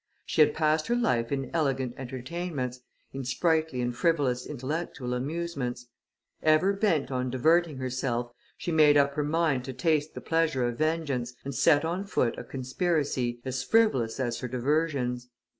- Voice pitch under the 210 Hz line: Yes, medium, 140 Hz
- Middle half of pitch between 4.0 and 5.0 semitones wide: Yes, average, 4.3 semitones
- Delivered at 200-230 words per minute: No, average, 160 wpm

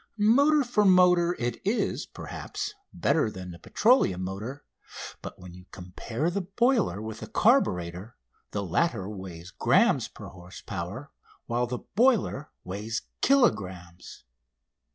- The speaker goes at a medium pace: No, slow, 130 wpm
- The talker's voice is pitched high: No, low, 120 Hz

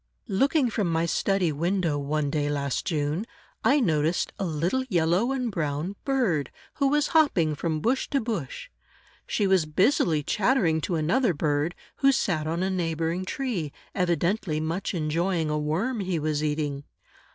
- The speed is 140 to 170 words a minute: Yes, average, 155 wpm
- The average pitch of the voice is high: No, medium, 170 Hz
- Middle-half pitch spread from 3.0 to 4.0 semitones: No, average, 5.1 semitones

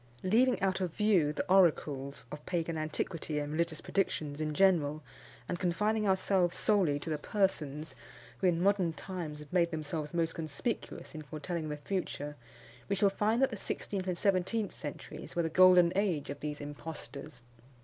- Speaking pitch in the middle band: Yes, medium, 170 Hz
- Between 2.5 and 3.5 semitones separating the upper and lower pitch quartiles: No, average, 4.1 semitones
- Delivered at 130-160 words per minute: No, average, 170 wpm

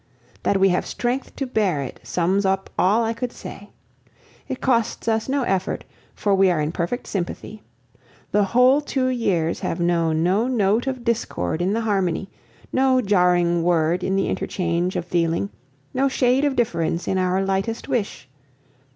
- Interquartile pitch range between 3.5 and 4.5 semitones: No, average, 5.3 semitones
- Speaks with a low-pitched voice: No, high, 195 Hz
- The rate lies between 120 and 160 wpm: No, average, 170 wpm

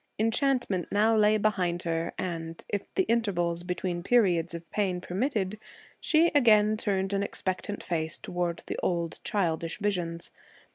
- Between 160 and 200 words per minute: No, average, 140 wpm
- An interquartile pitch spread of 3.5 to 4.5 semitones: Yes, average, 3.8 semitones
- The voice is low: No, high, 190 Hz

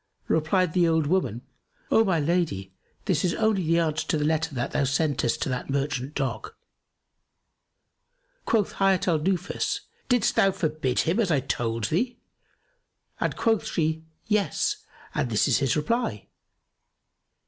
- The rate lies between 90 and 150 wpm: Yes, average, 145 wpm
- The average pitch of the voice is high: No, medium, 160 Hz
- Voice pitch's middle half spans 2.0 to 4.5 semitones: No, average, 5.3 semitones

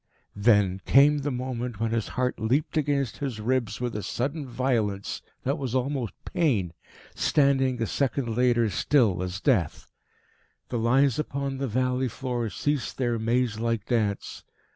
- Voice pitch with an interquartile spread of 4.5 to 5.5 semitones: No, average, 3.3 semitones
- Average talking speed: Yes, average, 150 wpm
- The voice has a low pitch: Yes, low, 125 Hz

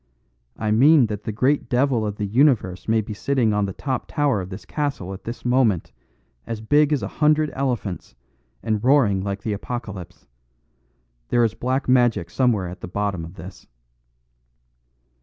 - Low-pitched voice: Yes, low, 110 Hz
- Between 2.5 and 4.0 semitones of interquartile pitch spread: No, average, 4.7 semitones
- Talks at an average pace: Yes, average, 170 wpm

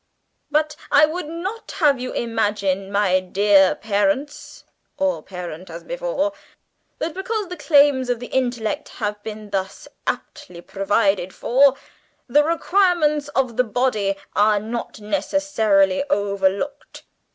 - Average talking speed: No, slow, 120 wpm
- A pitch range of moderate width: No, wide, 6.7 semitones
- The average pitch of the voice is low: No, high, 240 Hz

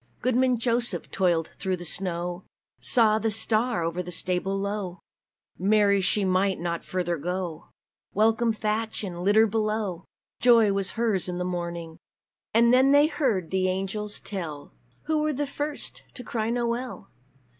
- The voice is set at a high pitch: Yes, high, 200 Hz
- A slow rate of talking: No, average, 150 wpm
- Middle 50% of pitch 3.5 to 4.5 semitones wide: Yes, average, 4.2 semitones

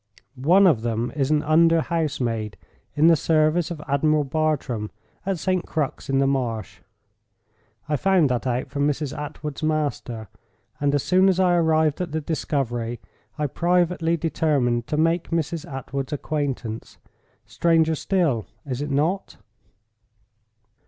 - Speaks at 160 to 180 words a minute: No, average, 140 wpm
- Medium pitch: Yes, medium, 150 Hz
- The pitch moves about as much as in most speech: Yes, average, 3.6 semitones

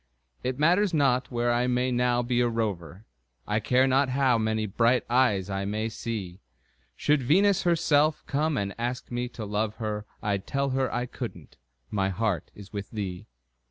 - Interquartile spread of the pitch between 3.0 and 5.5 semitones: Yes, average, 3.8 semitones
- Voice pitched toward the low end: Yes, low, 120 Hz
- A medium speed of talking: Yes, average, 175 wpm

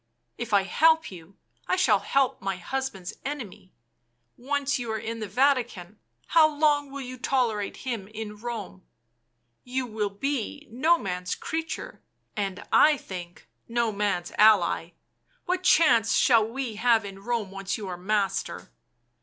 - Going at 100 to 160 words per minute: Yes, average, 150 wpm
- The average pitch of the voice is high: Yes, high, 225 Hz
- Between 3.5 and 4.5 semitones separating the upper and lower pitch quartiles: No, wide, 5.4 semitones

